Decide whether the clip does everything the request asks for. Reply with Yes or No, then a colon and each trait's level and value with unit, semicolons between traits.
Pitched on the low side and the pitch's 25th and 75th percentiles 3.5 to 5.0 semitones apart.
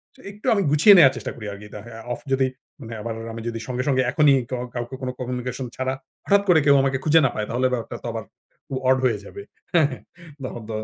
No: low, 130 Hz; average, 2.9 semitones